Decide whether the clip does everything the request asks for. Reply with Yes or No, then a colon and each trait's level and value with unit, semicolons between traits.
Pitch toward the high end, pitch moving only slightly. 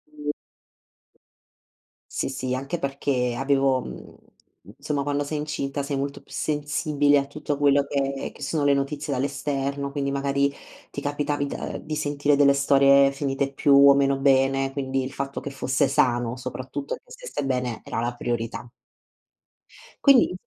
No: medium, 140 Hz; narrow, 1.1 semitones